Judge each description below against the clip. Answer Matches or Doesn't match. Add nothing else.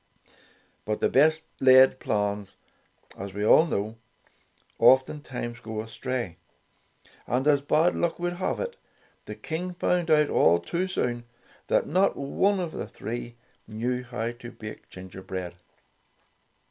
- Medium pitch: Doesn't match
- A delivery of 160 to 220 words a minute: Doesn't match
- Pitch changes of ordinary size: Doesn't match